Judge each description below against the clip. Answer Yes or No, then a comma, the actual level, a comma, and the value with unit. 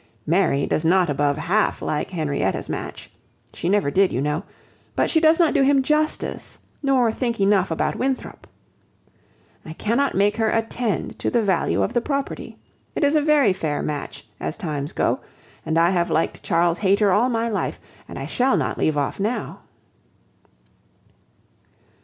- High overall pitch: Yes, high, 200 Hz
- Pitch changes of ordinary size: No, wide, 7.4 semitones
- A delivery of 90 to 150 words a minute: No, average, 165 wpm